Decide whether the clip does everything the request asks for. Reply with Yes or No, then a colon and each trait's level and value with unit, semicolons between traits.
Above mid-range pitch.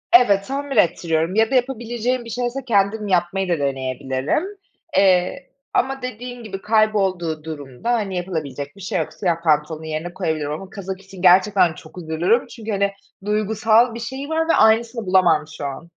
Yes: high, 195 Hz